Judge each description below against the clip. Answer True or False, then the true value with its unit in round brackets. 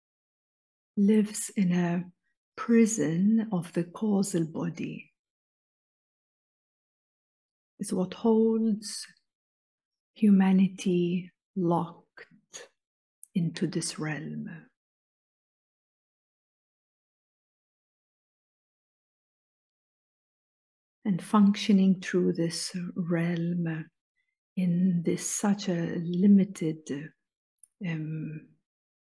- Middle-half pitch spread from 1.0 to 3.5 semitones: True (3.1 semitones)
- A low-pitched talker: False (185 Hz)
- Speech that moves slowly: True (55 wpm)